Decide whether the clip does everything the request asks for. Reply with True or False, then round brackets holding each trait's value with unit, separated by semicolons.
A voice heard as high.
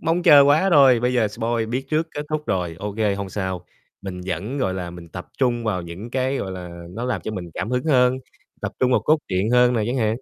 False (115 Hz)